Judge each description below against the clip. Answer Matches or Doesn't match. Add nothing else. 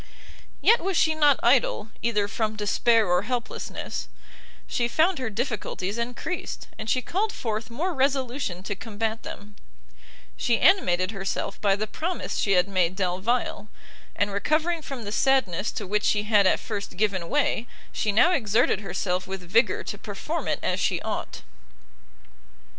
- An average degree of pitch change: Matches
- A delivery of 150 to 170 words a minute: Matches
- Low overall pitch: Doesn't match